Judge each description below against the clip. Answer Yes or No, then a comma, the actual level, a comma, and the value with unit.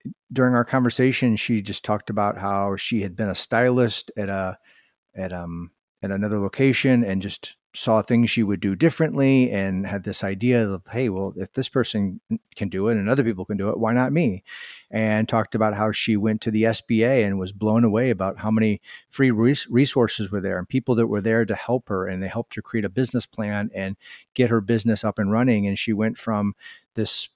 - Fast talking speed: Yes, fast, 215 wpm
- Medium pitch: No, low, 110 Hz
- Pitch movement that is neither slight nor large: Yes, average, 3.2 semitones